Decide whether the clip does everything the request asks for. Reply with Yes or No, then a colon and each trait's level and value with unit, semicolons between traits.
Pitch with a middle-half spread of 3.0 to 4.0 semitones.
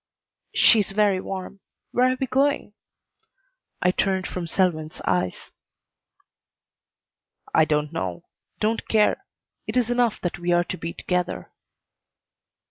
No: average, 4.5 semitones